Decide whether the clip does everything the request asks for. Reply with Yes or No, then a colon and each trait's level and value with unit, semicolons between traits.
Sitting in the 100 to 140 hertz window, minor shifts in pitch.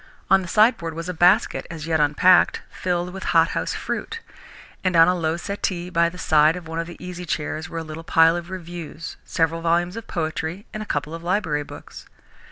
No: medium, 170 Hz; narrow, 1.9 semitones